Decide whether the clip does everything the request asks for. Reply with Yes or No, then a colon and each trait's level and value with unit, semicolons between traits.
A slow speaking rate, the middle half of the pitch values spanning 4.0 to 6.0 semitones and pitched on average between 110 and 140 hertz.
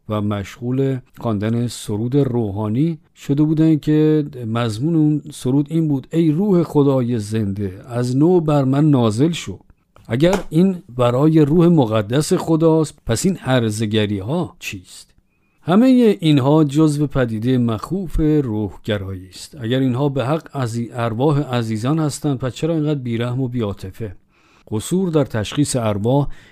No: average, 135 wpm; average, 5.2 semitones; low, 135 Hz